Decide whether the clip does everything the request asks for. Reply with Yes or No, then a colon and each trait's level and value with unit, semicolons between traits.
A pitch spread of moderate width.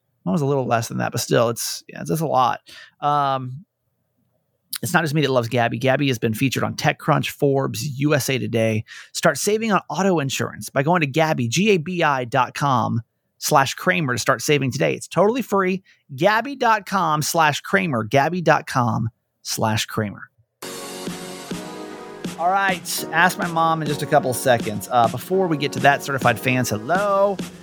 No: wide, 5.8 semitones